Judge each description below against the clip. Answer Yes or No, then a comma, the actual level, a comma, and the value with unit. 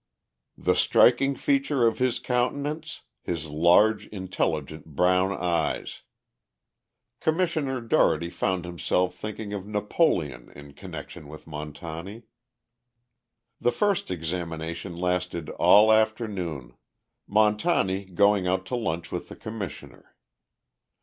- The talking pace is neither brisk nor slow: No, slow, 105 wpm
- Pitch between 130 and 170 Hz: No, very low, 95 Hz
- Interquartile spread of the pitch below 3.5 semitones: No, average, 5.2 semitones